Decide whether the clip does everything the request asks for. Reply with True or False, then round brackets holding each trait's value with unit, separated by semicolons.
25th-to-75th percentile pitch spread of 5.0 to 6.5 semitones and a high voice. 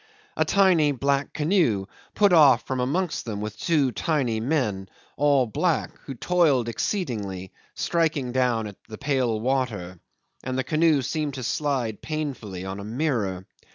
False (5.6 semitones; 130 Hz)